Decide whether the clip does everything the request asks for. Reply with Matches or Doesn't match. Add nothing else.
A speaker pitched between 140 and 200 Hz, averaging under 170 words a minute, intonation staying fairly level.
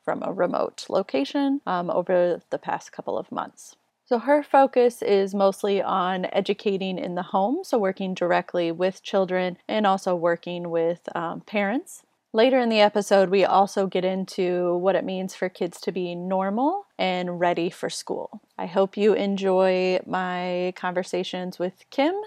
Matches